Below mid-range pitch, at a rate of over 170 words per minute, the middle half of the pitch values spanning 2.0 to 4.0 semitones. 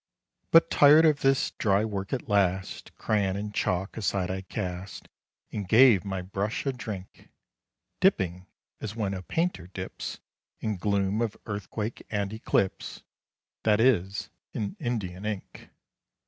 No: low, 100 Hz; slow, 135 wpm; average, 2.8 semitones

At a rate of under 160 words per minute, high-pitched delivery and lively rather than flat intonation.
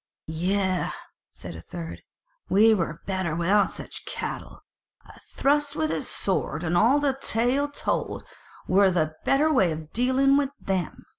Yes: average, 150 wpm; high, 200 Hz; wide, 7.8 semitones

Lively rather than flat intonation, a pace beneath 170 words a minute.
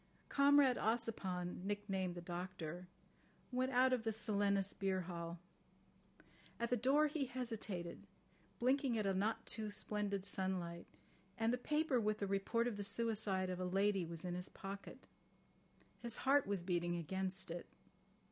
No: average, 4.1 semitones; average, 145 wpm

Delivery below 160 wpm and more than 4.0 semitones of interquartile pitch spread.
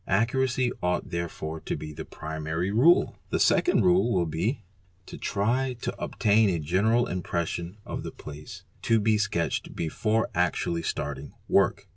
Yes: average, 145 wpm; wide, 5.6 semitones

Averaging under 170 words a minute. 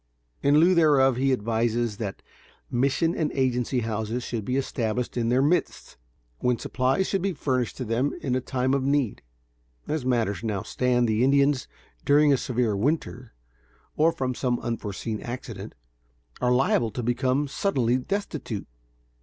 Yes: average, 155 wpm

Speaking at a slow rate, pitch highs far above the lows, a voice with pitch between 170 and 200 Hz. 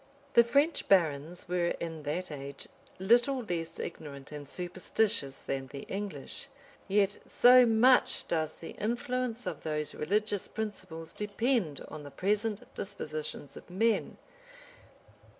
Yes: slow, 125 wpm; wide, 6.3 semitones; medium, 185 Hz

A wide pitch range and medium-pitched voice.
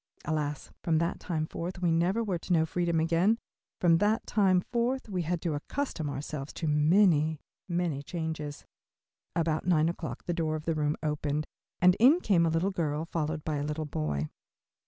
No: average, 2.8 semitones; medium, 165 Hz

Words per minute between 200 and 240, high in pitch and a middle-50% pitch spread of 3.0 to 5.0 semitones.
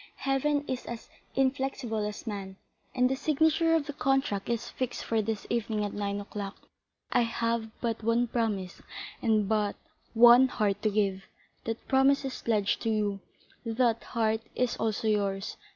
No: average, 160 wpm; high, 225 Hz; average, 3.4 semitones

